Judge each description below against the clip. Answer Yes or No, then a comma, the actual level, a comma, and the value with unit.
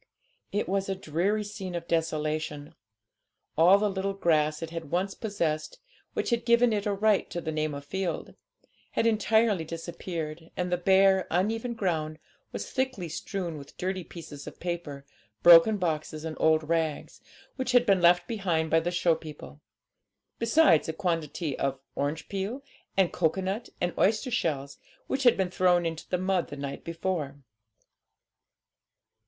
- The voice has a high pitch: No, medium, 175 Hz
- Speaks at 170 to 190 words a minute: No, average, 160 wpm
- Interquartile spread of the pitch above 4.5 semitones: No, average, 3.8 semitones